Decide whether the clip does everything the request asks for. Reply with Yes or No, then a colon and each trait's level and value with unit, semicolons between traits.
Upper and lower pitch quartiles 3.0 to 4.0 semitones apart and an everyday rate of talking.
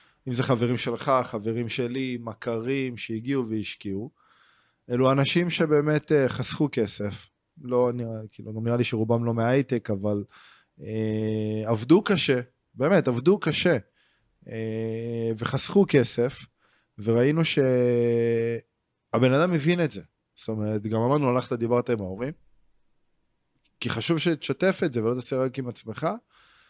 Yes: average, 3.4 semitones; average, 130 wpm